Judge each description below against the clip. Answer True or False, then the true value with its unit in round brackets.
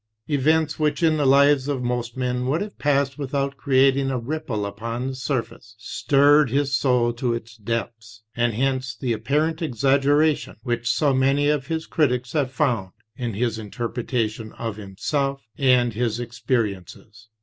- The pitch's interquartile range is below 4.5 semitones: True (3.4 semitones)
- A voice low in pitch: True (130 Hz)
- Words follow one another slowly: False (155 wpm)